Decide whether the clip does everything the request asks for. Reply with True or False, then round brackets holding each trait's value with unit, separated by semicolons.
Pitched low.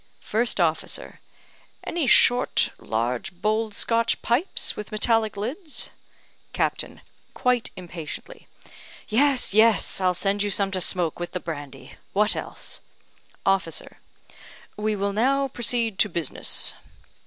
False (210 Hz)